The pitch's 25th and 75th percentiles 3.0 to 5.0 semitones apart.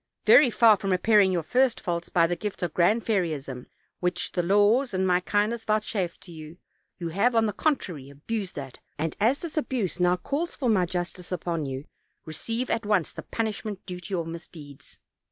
Yes: average, 4.7 semitones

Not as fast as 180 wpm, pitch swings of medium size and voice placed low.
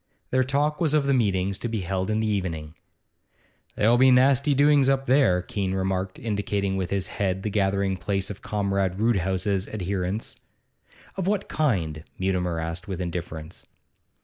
Yes: average, 160 wpm; average, 4.6 semitones; low, 100 Hz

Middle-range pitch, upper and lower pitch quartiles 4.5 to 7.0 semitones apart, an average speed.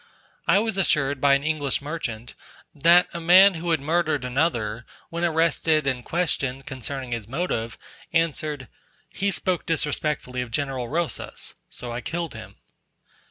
Yes: medium, 150 Hz; average, 4.8 semitones; average, 145 wpm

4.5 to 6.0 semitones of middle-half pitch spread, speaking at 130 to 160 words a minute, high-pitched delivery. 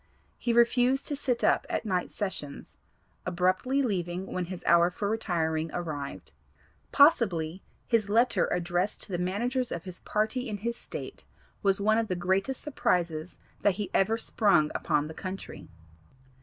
Yes: average, 4.8 semitones; average, 155 wpm; high, 195 Hz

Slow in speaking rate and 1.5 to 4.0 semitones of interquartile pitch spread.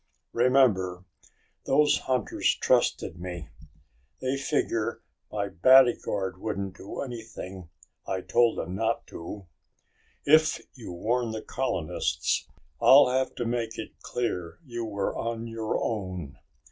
No: slow, 120 wpm; average, 4.8 semitones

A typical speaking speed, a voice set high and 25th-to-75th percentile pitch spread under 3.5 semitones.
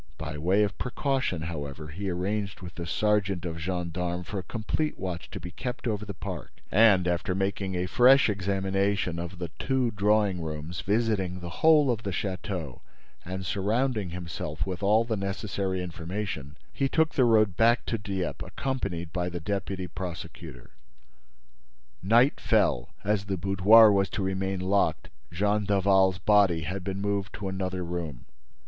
No: average, 160 wpm; very low, 95 Hz; average, 3.1 semitones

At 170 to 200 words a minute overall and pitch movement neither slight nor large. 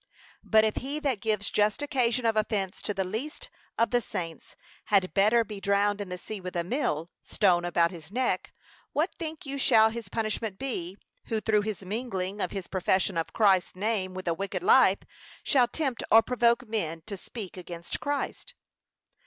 Yes: average, 185 wpm; average, 4.0 semitones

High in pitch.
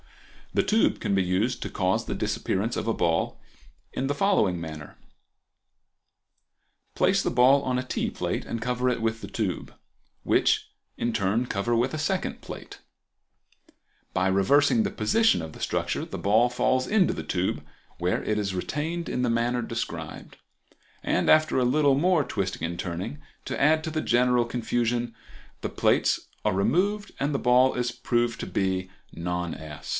No: low, 120 Hz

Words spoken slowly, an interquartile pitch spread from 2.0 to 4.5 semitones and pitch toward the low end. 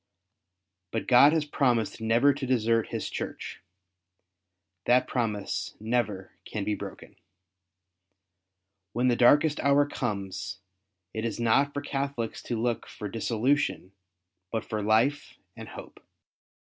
Yes: slow, 120 wpm; average, 4.1 semitones; low, 120 Hz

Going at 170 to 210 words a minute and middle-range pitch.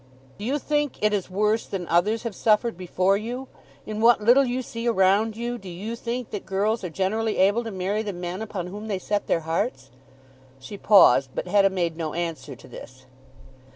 No: average, 200 wpm; high, 205 Hz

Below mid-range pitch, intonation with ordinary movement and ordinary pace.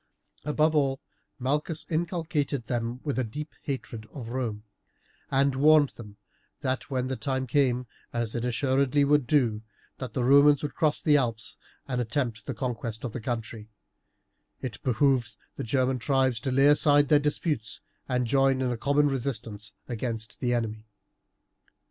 Yes: low, 130 Hz; average, 3.3 semitones; average, 160 wpm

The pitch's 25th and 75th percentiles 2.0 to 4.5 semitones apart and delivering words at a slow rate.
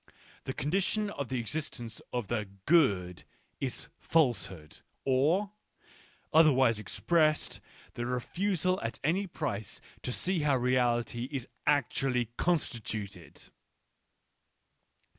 No: wide, 5.4 semitones; slow, 105 wpm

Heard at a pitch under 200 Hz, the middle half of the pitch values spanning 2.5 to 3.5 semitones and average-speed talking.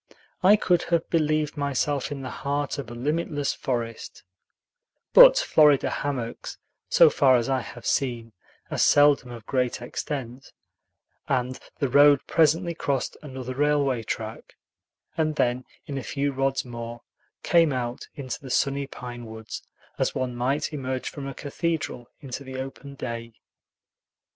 Yes: low, 135 Hz; average, 2.9 semitones; average, 145 wpm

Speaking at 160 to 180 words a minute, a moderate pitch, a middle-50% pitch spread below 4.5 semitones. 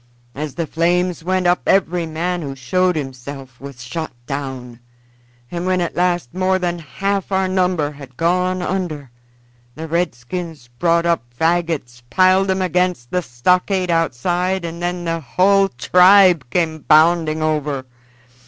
No: average, 145 wpm; medium, 170 Hz; average, 3.9 semitones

